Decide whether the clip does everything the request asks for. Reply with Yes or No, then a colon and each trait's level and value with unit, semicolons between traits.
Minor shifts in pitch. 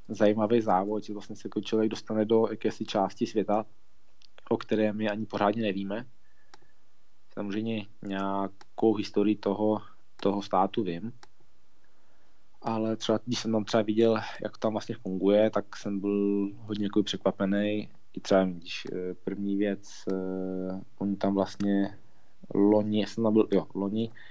Yes: narrow, 1.8 semitones